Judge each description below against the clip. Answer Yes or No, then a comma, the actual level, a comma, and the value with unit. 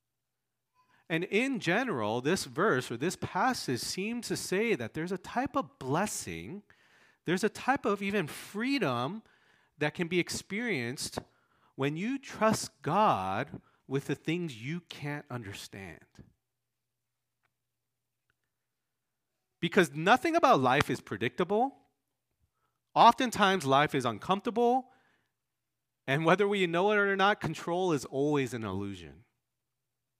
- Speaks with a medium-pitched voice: Yes, medium, 160 Hz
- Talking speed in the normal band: No, slow, 115 wpm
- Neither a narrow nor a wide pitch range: No, wide, 8.8 semitones